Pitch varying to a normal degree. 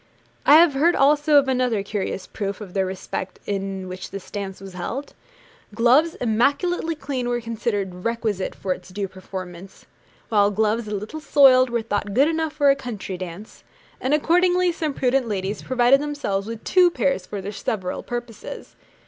No: wide, 6.1 semitones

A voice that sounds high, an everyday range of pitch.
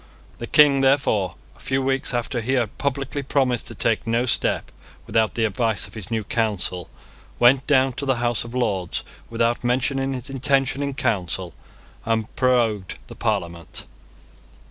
No: low, 120 Hz; average, 3.3 semitones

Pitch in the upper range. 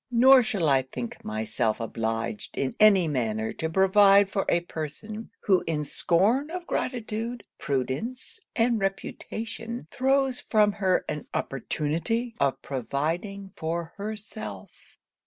Yes: high, 195 Hz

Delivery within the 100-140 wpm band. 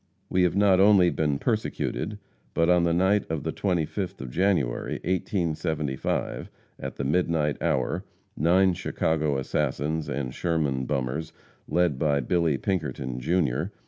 Yes: slow, 135 wpm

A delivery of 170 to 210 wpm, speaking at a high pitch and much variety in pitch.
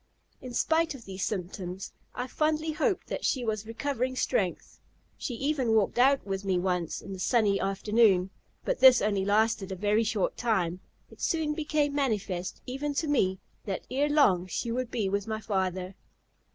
Yes: average, 175 wpm; high, 220 Hz; wide, 6.0 semitones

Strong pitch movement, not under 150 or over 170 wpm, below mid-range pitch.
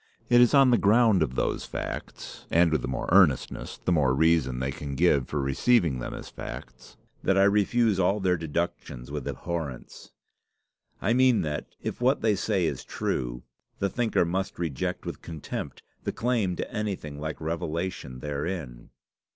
Yes: wide, 6.2 semitones; average, 165 wpm; very low, 85 Hz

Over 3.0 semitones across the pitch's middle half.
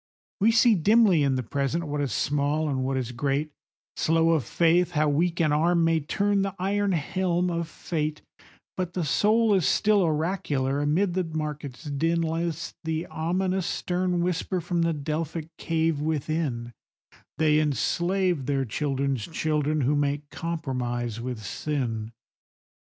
Yes: average, 3.5 semitones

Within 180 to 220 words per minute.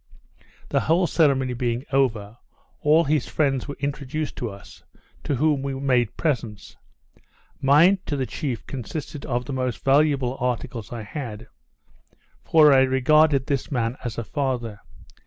No: average, 145 wpm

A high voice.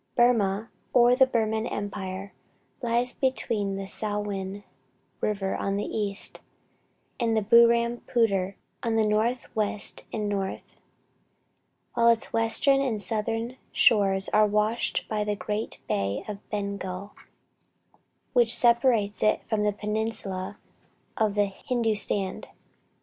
Yes: high, 215 Hz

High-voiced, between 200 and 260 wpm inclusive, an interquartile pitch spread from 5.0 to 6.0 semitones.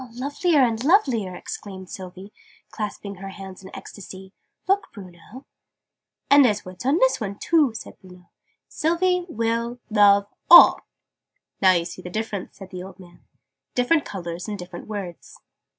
No: high, 205 Hz; average, 150 wpm; average, 5.3 semitones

